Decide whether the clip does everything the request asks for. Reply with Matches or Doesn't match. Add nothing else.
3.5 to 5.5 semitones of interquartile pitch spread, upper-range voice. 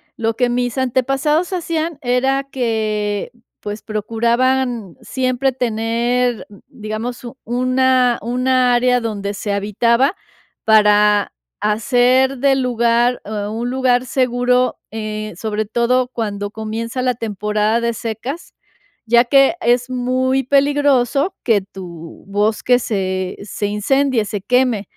Doesn't match